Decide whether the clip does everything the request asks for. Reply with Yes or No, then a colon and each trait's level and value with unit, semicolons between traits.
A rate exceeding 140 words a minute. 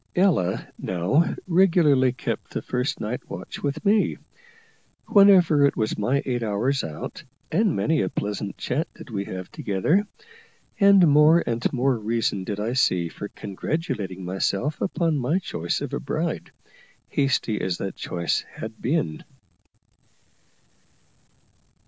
No: slow, 135 wpm